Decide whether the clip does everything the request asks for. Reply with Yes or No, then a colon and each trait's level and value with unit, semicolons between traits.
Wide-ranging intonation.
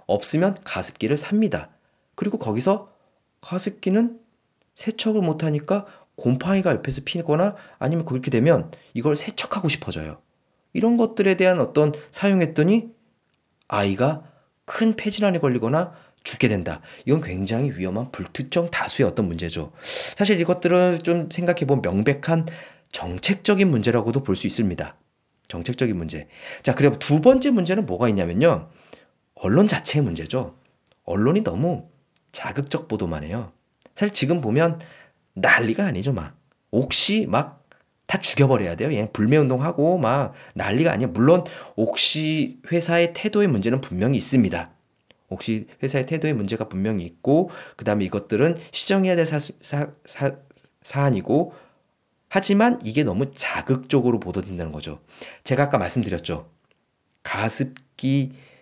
Yes: wide, 7.7 semitones